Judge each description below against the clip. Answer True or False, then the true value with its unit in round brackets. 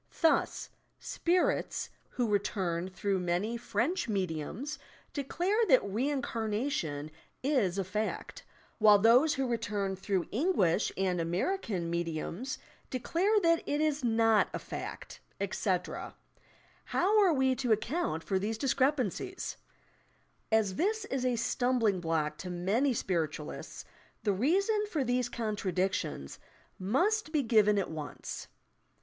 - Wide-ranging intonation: True (7.2 semitones)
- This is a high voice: True (225 Hz)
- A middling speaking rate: False (125 wpm)